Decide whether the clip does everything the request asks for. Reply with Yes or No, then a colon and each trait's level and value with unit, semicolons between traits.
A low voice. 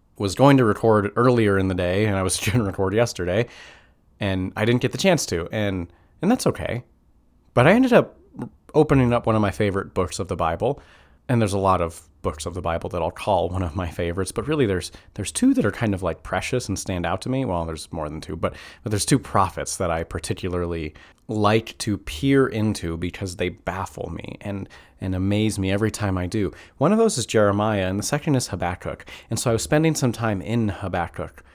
Yes: low, 100 Hz